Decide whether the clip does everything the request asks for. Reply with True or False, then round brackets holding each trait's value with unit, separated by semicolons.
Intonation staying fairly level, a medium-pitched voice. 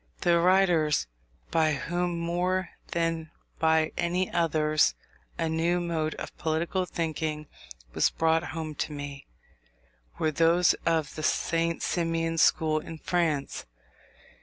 True (1.6 semitones; 165 Hz)